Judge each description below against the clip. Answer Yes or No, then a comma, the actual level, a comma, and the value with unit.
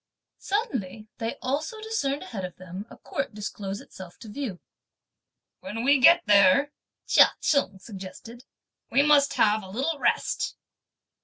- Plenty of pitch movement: Yes, wide, 6.3 semitones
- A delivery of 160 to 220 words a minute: No, average, 140 wpm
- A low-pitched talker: No, high, 230 Hz